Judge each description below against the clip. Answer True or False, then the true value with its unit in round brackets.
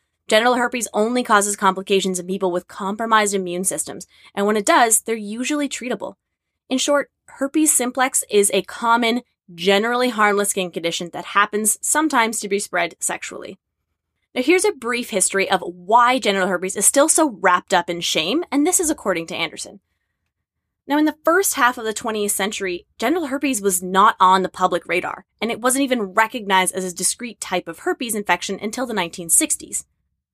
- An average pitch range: True (4.9 semitones)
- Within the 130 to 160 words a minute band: False (180 wpm)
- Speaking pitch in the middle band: False (210 Hz)